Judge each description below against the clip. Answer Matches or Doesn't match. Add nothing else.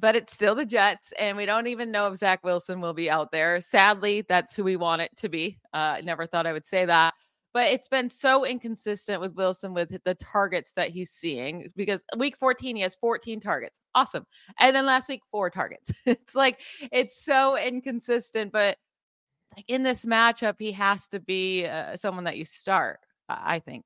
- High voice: Matches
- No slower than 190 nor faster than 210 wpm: Matches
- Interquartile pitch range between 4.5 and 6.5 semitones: Matches